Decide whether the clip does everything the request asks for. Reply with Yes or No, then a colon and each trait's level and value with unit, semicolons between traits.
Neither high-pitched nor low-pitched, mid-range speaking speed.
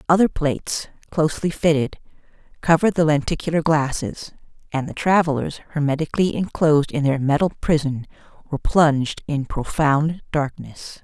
No: medium, 150 Hz; slow, 120 wpm